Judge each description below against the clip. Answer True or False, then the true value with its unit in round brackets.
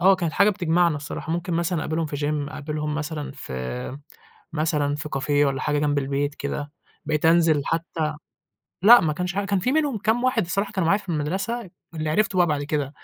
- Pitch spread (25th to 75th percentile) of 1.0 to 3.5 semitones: False (3.9 semitones)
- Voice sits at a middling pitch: True (155 Hz)